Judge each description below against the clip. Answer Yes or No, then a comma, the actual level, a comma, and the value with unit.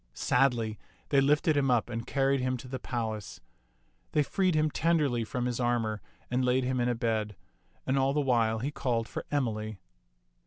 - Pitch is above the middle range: No, low, 125 Hz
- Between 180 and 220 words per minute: Yes, average, 185 wpm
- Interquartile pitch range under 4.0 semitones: Yes, average, 3.1 semitones